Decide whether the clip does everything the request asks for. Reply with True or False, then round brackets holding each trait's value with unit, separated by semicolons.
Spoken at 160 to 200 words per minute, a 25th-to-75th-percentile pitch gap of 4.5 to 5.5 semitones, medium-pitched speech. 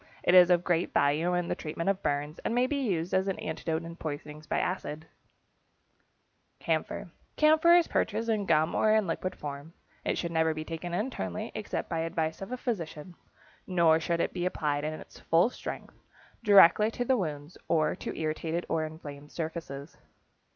False (180 wpm; 3.6 semitones; 165 Hz)